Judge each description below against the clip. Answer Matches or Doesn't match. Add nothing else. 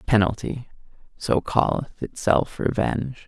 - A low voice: Matches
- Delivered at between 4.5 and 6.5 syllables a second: Doesn't match